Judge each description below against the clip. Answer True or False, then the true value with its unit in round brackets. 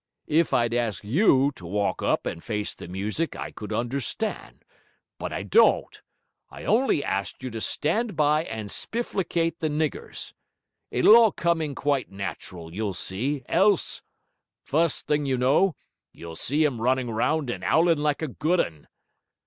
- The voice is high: False (140 Hz)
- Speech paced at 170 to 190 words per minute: False (160 wpm)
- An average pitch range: False (6.8 semitones)